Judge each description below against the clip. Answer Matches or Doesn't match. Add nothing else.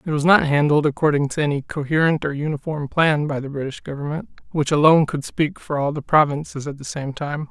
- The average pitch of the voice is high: Doesn't match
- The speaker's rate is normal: Doesn't match